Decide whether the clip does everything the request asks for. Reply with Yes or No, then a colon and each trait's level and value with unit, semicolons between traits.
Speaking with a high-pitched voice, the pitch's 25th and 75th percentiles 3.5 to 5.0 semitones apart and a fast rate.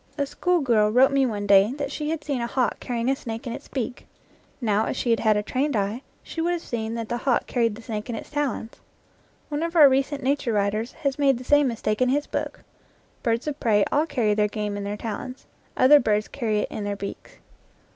Yes: high, 240 Hz; average, 4.6 semitones; fast, 235 wpm